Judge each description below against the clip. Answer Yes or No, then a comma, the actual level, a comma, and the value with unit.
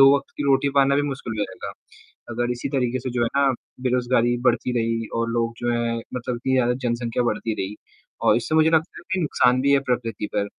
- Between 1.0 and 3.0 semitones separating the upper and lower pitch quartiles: Yes, narrow, 2.6 semitones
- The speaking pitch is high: No, low, 125 Hz